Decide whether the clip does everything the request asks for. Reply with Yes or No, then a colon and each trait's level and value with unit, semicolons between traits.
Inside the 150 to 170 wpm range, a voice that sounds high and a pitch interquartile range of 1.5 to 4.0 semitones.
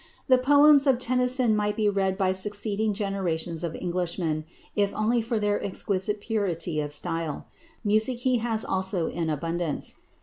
No: average, 155 wpm; high, 205 Hz; average, 4.4 semitones